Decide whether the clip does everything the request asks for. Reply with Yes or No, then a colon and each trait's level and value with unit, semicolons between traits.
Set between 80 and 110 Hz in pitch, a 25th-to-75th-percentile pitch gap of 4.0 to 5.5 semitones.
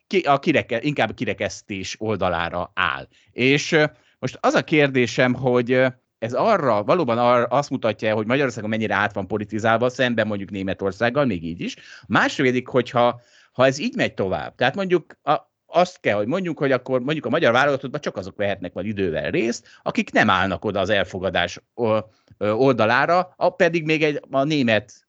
No: low, 125 Hz; average, 4.8 semitones